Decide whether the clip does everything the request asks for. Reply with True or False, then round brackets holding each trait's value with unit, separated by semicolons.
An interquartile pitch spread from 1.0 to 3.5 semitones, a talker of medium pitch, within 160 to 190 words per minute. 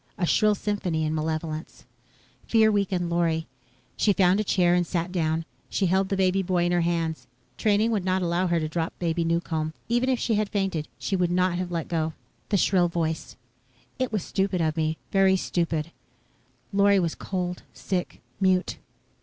True (2.7 semitones; 180 Hz; 180 wpm)